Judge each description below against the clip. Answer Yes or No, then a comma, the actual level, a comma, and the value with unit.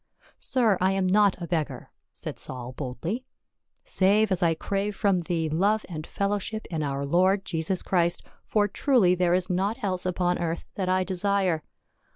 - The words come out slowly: No, average, 170 wpm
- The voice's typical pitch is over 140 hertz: Yes, medium, 185 Hz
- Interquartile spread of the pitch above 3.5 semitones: No, average, 2.8 semitones